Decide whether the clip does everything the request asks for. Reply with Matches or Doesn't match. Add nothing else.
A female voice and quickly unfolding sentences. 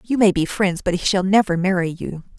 Matches